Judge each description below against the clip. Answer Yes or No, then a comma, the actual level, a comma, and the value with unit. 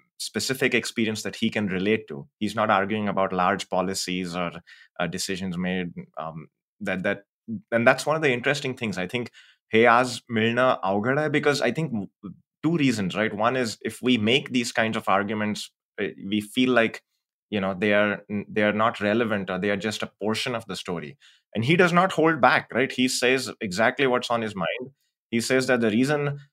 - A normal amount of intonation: Yes, average, 4.2 semitones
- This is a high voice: No, low, 110 Hz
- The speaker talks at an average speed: No, fast, 195 wpm